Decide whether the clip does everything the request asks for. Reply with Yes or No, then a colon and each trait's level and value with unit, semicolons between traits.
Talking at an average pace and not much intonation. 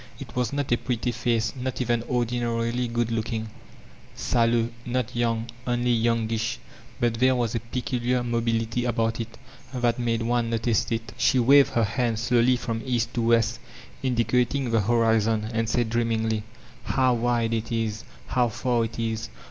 Yes: average, 165 wpm; narrow, 1.2 semitones